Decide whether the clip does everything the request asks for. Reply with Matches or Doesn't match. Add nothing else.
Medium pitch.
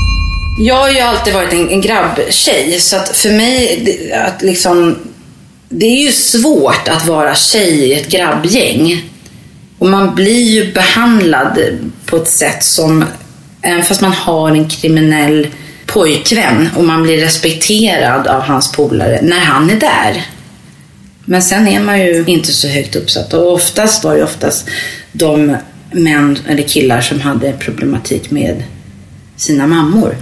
Matches